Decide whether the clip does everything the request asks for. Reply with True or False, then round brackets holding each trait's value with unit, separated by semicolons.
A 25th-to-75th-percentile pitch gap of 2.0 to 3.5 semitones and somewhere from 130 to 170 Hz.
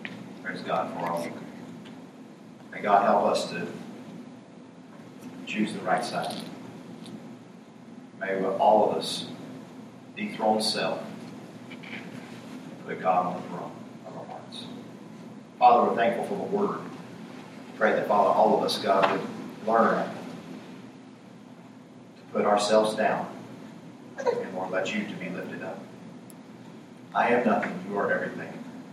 False (2.5 semitones; 105 Hz)